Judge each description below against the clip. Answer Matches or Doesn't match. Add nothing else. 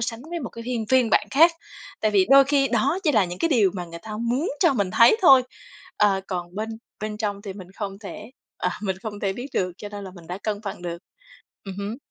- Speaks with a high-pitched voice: Matches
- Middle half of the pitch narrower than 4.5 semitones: Matches